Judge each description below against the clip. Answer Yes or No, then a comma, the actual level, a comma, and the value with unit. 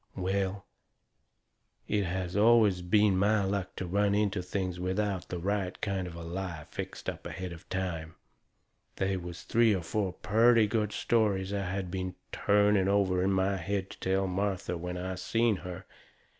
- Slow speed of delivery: No, average, 170 wpm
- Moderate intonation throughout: No, narrow, 2.0 semitones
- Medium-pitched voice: No, very low, 95 Hz